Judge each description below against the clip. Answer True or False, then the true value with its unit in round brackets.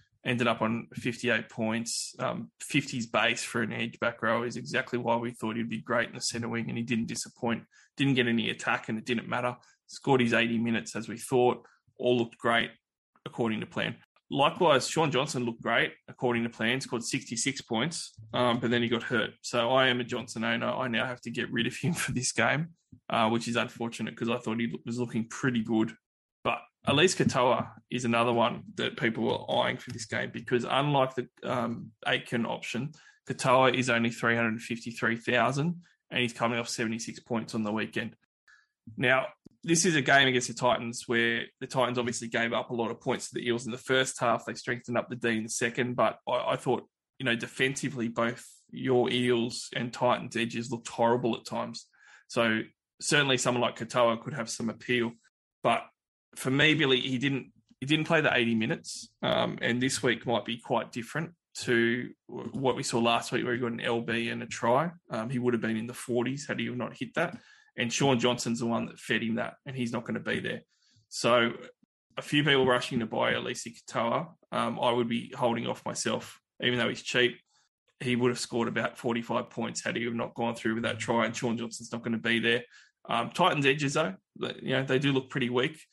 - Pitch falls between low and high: False (120 Hz)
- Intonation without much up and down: True (1.6 semitones)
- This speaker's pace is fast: True (215 wpm)